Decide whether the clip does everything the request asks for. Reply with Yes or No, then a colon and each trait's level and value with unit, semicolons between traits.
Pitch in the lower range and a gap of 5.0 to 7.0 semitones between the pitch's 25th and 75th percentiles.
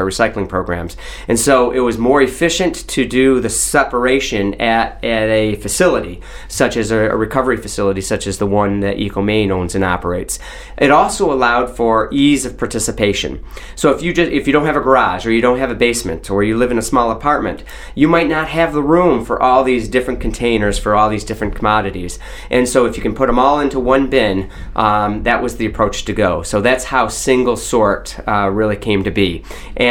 No: low, 115 Hz; average, 3.9 semitones